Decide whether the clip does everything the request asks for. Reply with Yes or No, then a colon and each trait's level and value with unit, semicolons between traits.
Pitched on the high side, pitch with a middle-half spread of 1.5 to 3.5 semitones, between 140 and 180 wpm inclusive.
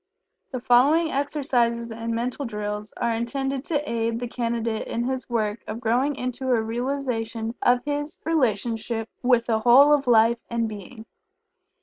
Yes: high, 235 Hz; average, 2.7 semitones; average, 150 wpm